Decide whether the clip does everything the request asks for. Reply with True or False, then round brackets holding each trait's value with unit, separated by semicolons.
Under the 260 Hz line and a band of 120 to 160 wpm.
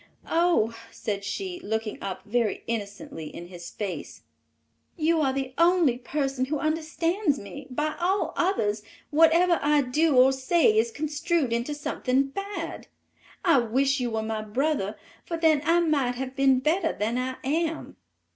False (275 Hz; 155 wpm)